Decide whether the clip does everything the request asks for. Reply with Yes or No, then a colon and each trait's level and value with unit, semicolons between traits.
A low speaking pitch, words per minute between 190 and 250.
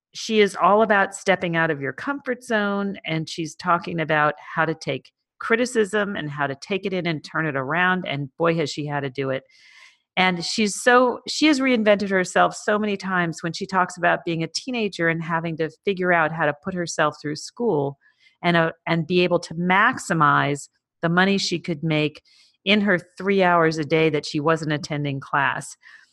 No: medium, 175 Hz; average, 200 wpm